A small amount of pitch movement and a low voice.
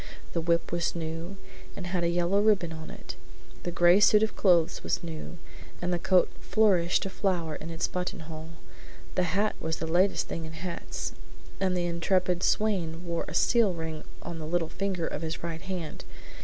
No: narrow, 2.3 semitones; medium, 175 Hz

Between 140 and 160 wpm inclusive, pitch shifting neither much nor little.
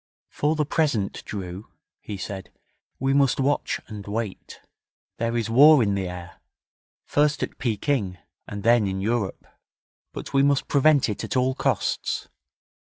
No: average, 150 wpm; wide, 5.8 semitones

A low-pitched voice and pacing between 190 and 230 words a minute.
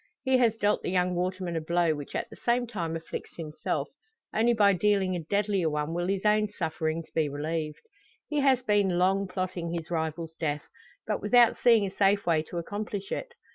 No: medium, 185 Hz; average, 195 wpm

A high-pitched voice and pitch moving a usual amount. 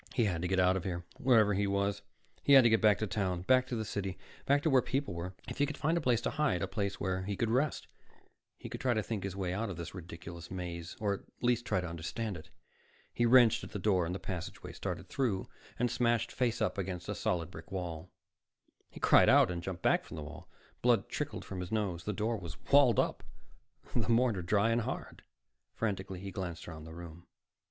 No: low, 100 Hz; average, 4.5 semitones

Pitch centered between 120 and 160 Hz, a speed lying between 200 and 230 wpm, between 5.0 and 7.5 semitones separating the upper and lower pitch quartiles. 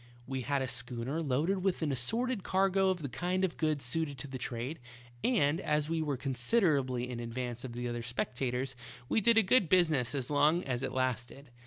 Yes: medium, 140 Hz; fast, 205 wpm; wide, 5.6 semitones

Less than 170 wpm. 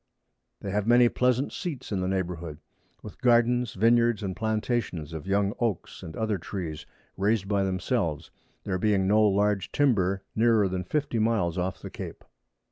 Yes: average, 160 wpm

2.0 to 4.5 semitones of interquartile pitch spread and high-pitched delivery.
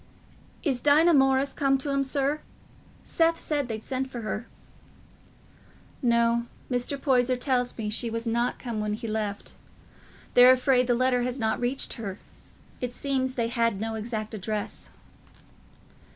Yes: average, 2.8 semitones; high, 245 Hz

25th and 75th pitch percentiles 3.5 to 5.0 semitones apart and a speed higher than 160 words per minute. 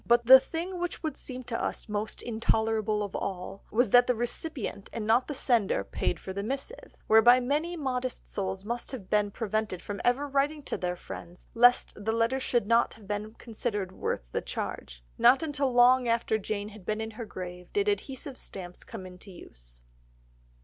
Yes: average, 4.2 semitones; average, 185 wpm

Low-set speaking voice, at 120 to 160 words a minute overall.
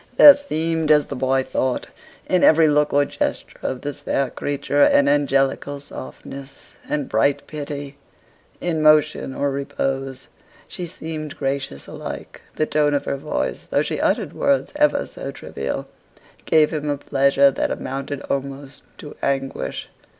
No: medium, 145 Hz; average, 150 wpm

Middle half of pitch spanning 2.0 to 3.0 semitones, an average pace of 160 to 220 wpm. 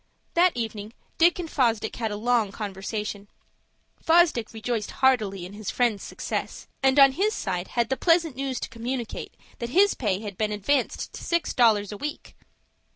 No: average, 4.6 semitones; average, 170 wpm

